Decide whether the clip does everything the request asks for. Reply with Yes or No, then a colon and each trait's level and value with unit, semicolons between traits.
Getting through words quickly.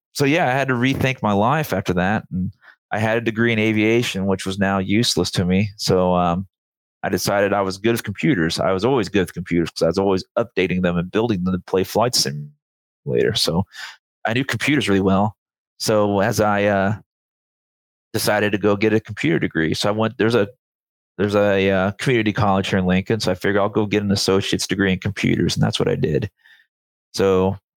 Yes: fast, 210 wpm